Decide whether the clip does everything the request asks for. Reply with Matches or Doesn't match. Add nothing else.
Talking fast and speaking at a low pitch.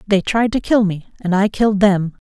Doesn't match